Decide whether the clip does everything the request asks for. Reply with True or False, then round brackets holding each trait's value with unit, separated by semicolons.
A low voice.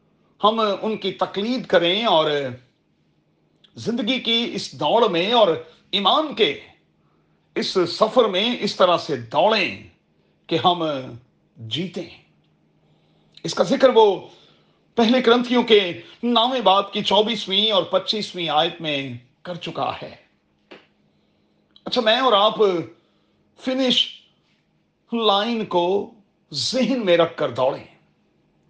False (200 Hz)